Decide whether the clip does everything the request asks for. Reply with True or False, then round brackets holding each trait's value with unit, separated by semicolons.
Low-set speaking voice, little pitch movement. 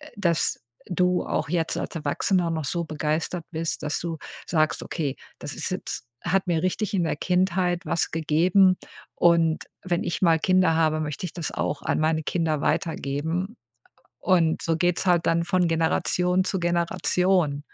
False (170 Hz; 2.2 semitones)